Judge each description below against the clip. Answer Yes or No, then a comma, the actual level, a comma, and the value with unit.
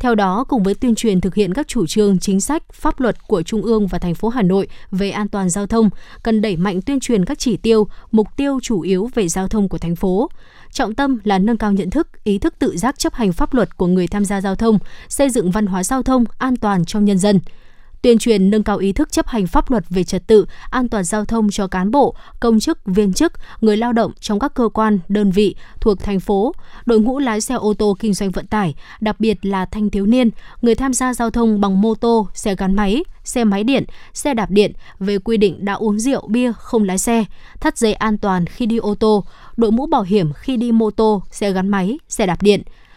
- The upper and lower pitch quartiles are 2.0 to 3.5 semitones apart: Yes, average, 3.0 semitones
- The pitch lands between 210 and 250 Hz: Yes, high, 215 Hz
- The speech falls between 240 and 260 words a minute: Yes, fast, 250 wpm